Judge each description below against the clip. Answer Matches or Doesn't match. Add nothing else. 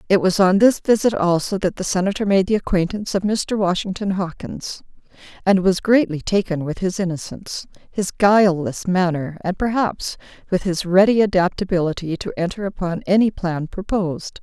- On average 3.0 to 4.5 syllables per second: Doesn't match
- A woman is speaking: Matches